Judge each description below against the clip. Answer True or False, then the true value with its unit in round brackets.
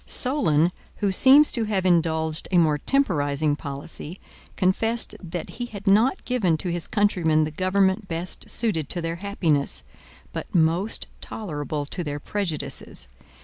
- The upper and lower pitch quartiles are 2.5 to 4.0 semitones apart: False (4.6 semitones)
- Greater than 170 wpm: False (145 wpm)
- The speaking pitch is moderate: True (175 Hz)